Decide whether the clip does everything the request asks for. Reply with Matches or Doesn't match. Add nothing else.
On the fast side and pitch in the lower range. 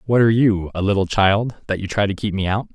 Matches